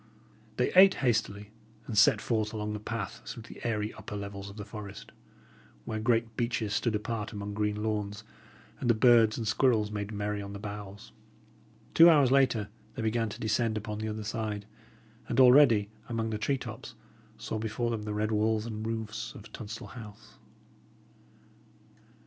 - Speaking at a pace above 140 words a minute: Yes, average, 170 wpm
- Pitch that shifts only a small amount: Yes, narrow, 1.8 semitones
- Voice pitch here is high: No, low, 110 Hz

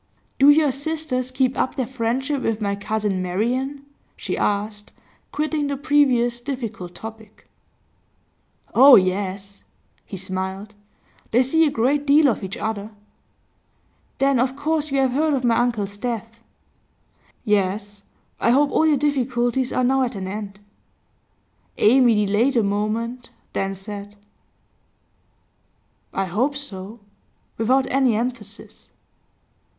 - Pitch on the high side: Yes, high, 240 Hz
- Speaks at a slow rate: Yes, slow, 125 wpm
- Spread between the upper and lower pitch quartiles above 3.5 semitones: Yes, average, 4.7 semitones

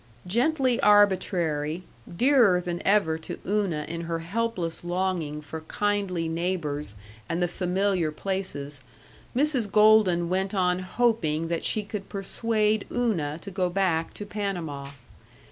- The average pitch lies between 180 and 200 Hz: Yes, medium, 185 Hz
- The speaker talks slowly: Yes, slow, 130 wpm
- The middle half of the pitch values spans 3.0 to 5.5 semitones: Yes, average, 3.9 semitones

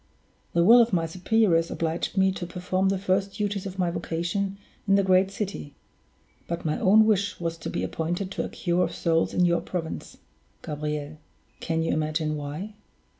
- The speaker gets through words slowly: No, average, 180 wpm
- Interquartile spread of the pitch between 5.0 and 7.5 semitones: No, average, 3.0 semitones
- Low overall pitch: No, medium, 180 Hz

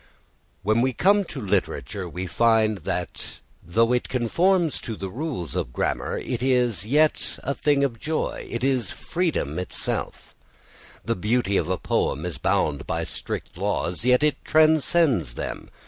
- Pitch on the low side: Yes, low, 120 Hz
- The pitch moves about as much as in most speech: No, wide, 7.4 semitones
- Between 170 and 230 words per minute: No, average, 150 wpm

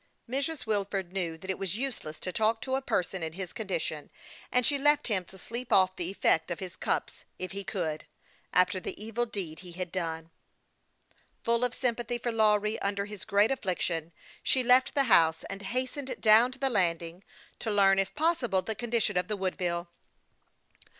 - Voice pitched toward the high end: Yes, high, 200 Hz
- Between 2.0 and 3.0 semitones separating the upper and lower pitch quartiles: No, average, 4.9 semitones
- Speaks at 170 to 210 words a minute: Yes, average, 190 wpm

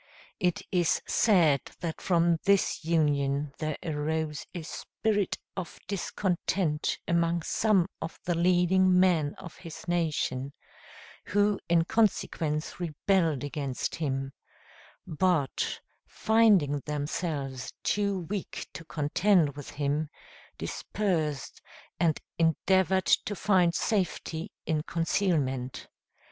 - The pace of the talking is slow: Yes, slow, 105 wpm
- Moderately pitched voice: Yes, medium, 165 Hz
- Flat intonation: No, average, 3.9 semitones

